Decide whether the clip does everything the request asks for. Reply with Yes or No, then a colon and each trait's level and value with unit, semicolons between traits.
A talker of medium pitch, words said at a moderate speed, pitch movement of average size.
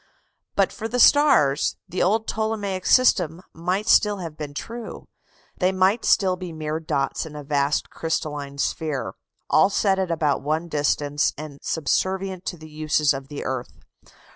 Yes: medium, 165 Hz; average, 160 wpm; average, 4.5 semitones